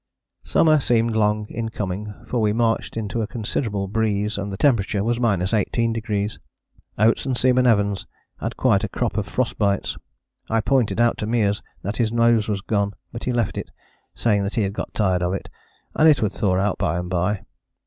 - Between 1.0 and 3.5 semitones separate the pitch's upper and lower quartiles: Yes, narrow, 2.6 semitones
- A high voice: No, low, 105 Hz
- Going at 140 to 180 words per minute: No, average, 195 wpm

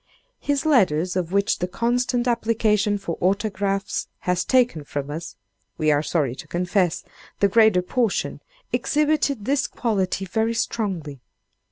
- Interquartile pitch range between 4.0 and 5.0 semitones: Yes, average, 4.7 semitones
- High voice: Yes, high, 200 Hz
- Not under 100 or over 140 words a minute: Yes, slow, 135 wpm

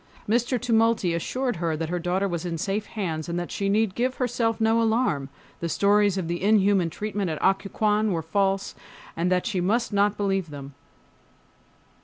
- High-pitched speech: Yes, high, 195 Hz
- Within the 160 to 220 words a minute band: Yes, average, 175 wpm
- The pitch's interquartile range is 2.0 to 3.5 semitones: No, average, 4.1 semitones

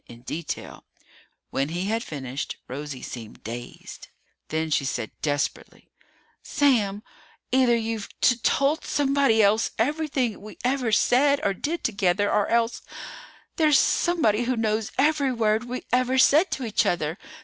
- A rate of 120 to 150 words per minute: Yes, average, 140 wpm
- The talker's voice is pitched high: Yes, high, 225 Hz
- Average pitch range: No, wide, 7.0 semitones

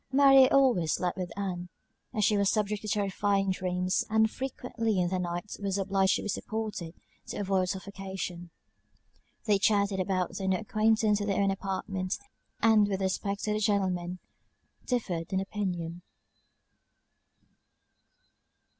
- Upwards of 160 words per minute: No, average, 140 wpm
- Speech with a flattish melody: Yes, narrow, 2.3 semitones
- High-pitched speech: Yes, high, 195 Hz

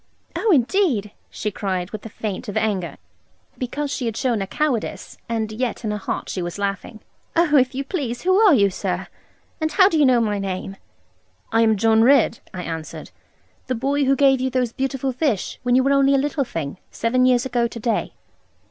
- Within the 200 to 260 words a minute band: Yes, fast, 205 wpm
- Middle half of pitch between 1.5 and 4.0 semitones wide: No, average, 4.6 semitones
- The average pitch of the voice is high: Yes, high, 245 Hz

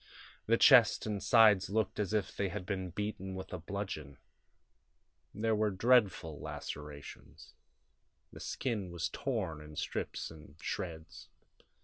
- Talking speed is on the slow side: Yes, slow, 130 wpm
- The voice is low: Yes, very low, 95 Hz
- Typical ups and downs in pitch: Yes, average, 4.5 semitones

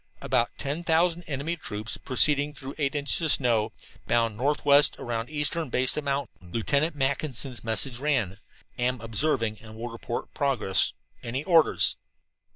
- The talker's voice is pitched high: No, low, 135 Hz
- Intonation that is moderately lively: Yes, average, 4.2 semitones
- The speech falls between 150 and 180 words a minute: No, average, 140 wpm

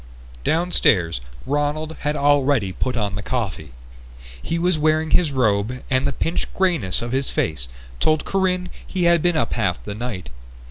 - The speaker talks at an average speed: Yes, average, 165 wpm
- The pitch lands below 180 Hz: Yes, medium, 140 Hz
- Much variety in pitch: Yes, wide, 7.4 semitones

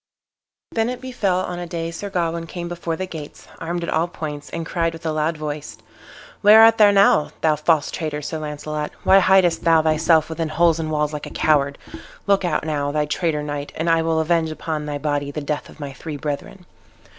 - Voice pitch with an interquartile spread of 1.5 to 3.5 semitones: Yes, narrow, 2.4 semitones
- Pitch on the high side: No, medium, 160 Hz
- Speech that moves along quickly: Yes, fast, 215 wpm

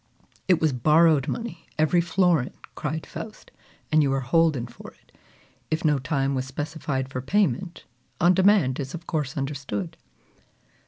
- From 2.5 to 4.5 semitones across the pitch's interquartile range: Yes, average, 4.1 semitones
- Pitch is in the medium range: Yes, medium, 155 Hz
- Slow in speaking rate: No, average, 150 wpm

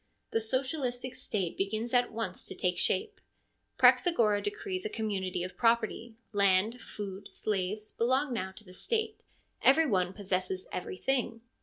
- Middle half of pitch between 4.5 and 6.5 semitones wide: Yes, average, 5.1 semitones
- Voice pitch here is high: Yes, high, 220 Hz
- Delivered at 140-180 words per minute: Yes, average, 150 wpm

